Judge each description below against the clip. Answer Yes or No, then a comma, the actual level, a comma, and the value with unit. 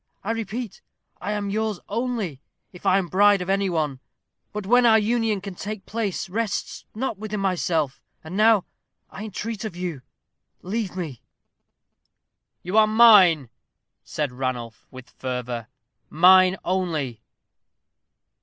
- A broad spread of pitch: No, average, 4.8 semitones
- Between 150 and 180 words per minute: No, slow, 135 wpm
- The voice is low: No, high, 195 Hz